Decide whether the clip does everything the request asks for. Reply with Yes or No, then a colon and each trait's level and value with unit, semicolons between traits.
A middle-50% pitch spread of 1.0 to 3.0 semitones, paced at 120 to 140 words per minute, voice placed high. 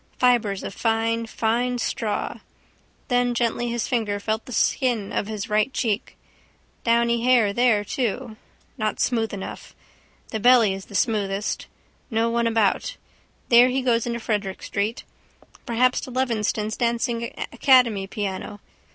Yes: narrow, 2.4 semitones; slow, 135 wpm; high, 230 Hz